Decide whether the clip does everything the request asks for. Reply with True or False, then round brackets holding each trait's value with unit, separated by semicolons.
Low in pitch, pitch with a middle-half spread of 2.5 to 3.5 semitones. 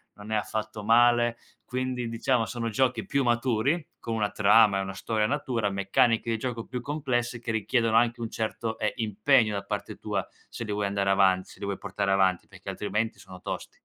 True (110 Hz; 2.8 semitones)